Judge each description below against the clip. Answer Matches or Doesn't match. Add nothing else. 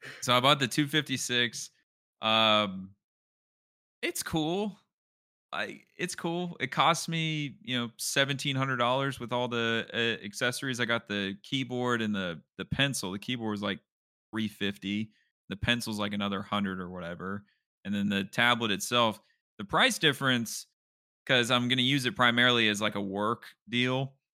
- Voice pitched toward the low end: Matches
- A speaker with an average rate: Matches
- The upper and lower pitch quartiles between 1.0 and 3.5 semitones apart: Doesn't match